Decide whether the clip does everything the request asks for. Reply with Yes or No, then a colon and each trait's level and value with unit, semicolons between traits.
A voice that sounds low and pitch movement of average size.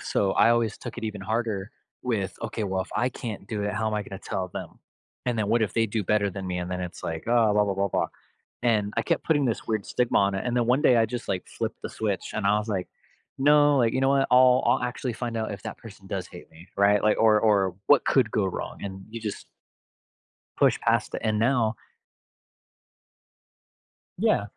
Yes: low, 110 Hz; average, 3.1 semitones